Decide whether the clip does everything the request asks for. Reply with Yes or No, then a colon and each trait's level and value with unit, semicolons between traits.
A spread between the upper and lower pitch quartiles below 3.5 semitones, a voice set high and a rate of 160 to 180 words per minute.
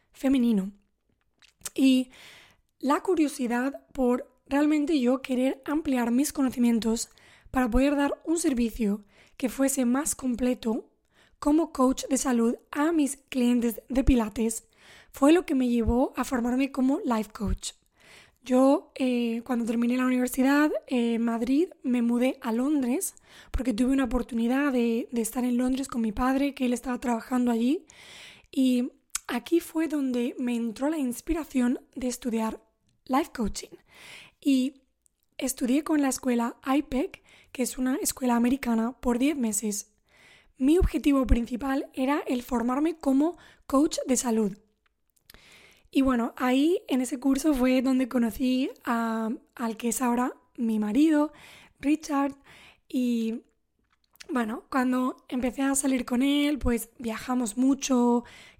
No: average, 2.7 semitones; very high, 260 Hz; slow, 135 wpm